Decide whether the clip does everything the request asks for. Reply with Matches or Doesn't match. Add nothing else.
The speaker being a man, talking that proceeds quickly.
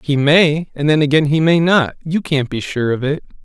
Matches